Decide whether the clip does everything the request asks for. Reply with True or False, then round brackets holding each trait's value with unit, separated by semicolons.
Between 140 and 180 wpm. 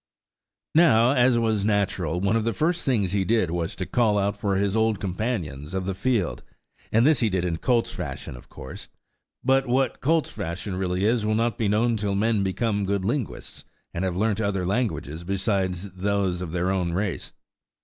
False (190 wpm)